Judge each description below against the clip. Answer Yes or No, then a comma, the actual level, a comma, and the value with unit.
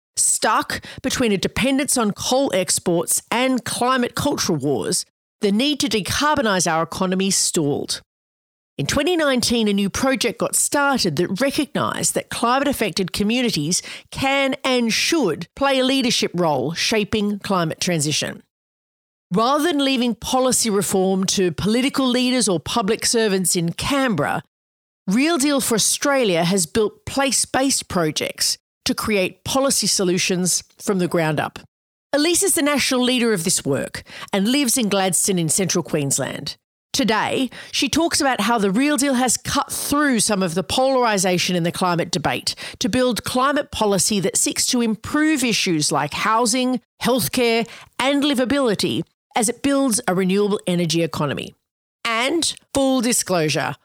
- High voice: Yes, high, 225 Hz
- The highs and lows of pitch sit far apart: Yes, wide, 6.1 semitones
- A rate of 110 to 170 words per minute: Yes, average, 145 wpm